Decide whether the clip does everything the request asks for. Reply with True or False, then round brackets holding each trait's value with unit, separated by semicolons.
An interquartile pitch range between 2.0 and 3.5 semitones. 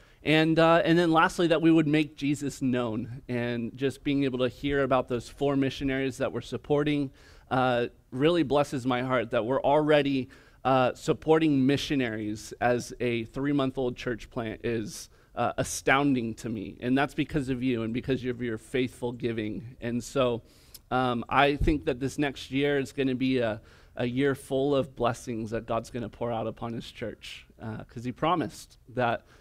True (2.9 semitones)